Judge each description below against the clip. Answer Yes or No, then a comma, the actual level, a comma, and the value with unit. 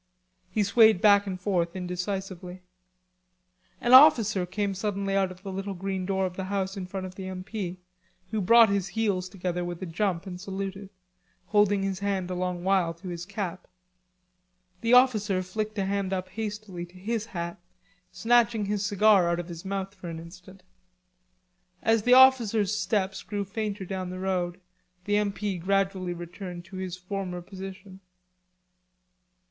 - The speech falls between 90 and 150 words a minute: No, average, 165 wpm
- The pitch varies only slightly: Yes, narrow, 2.1 semitones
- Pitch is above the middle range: Yes, high, 195 Hz